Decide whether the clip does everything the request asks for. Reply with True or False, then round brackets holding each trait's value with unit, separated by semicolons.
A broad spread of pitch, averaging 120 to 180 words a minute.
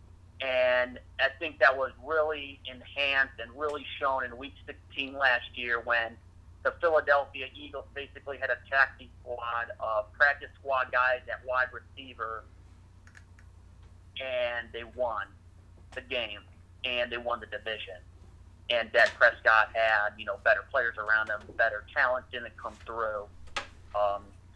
True (6.1 semitones; 140 wpm)